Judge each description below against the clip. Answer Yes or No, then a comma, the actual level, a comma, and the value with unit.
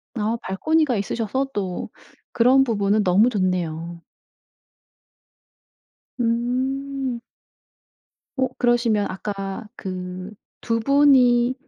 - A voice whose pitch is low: No, high, 230 Hz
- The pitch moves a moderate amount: Yes, average, 4.7 semitones